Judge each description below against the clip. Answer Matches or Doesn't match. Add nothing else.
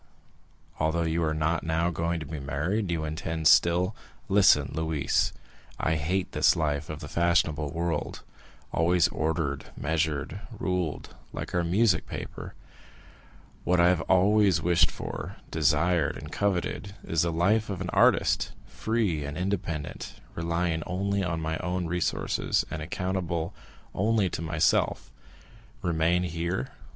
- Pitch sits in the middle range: Doesn't match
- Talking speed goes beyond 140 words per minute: Doesn't match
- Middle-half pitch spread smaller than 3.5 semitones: Matches